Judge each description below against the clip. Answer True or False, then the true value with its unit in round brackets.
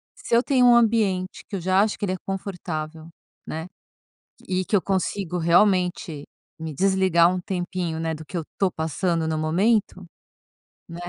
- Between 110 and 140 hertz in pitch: False (185 Hz)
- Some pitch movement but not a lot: True (3.0 semitones)